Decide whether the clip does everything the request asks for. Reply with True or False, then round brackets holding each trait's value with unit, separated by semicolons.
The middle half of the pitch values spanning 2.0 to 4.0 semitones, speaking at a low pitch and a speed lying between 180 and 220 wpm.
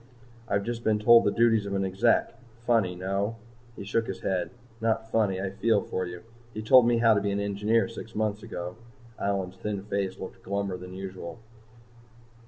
True (2.8 semitones; 100 Hz; 190 wpm)